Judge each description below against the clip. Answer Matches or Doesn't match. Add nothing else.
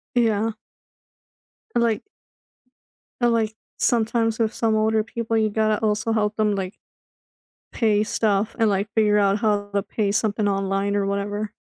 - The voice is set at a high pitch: Matches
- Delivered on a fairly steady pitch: Matches